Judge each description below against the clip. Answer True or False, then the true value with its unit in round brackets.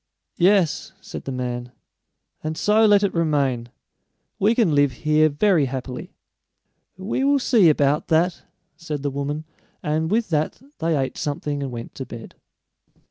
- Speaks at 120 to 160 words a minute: True (150 wpm)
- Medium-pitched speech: True (155 Hz)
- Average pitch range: True (5.0 semitones)